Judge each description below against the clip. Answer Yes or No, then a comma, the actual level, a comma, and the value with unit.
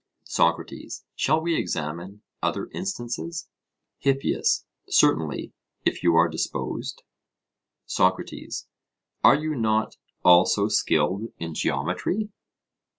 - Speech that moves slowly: Yes, slow, 90 wpm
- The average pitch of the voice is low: Yes, low, 110 Hz